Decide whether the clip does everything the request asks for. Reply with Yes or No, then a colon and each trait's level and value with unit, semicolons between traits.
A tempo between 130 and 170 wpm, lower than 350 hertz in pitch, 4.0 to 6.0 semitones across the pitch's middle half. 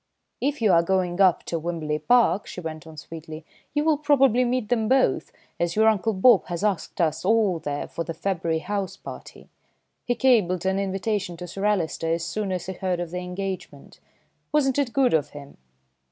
No: average, 195 wpm; high, 190 Hz; average, 4.9 semitones